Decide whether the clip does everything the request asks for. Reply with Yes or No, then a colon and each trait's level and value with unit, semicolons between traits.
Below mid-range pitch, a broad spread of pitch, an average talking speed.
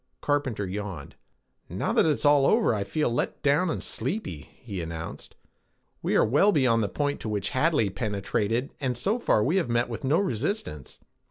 Yes: low, 120 Hz; wide, 6.2 semitones; average, 180 wpm